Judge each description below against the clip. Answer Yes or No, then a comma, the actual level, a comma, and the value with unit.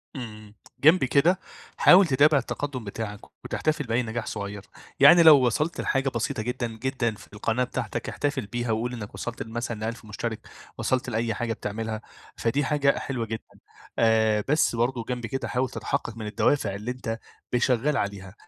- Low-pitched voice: Yes, low, 120 Hz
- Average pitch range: Yes, average, 3.3 semitones